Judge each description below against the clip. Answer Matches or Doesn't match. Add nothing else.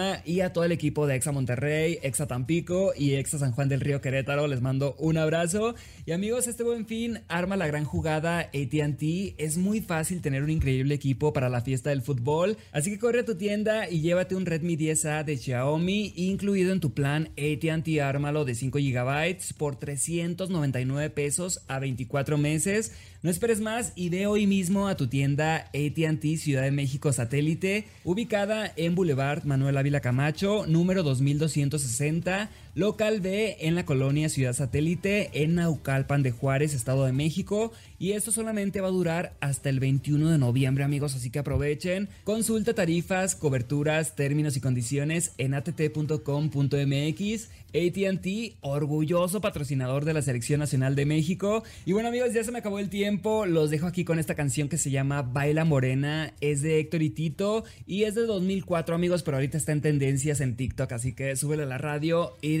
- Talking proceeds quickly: Doesn't match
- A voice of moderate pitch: Matches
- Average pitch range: Matches